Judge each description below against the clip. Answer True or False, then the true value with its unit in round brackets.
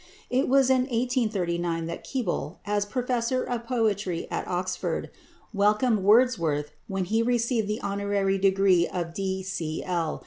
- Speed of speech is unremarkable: False (130 wpm)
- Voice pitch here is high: True (200 Hz)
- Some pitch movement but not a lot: True (4.7 semitones)